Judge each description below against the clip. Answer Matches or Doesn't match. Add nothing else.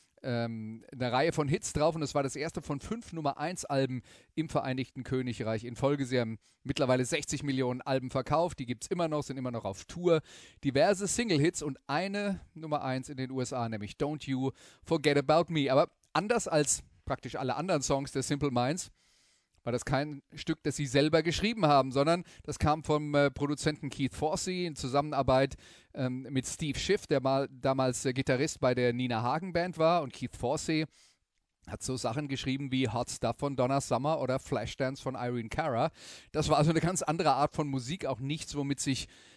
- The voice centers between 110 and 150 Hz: Matches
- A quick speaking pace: Matches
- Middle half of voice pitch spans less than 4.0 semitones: Matches